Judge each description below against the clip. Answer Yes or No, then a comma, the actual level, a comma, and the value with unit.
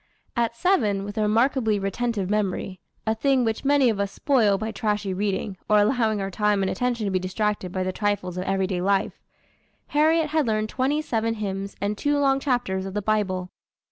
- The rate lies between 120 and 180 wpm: No, average, 200 wpm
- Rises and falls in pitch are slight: No, average, 3.8 semitones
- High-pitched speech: Yes, high, 210 Hz